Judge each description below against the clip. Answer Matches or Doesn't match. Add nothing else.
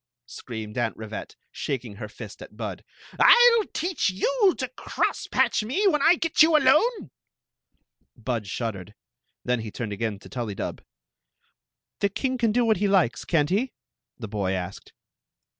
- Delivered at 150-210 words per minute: Matches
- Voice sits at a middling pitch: Matches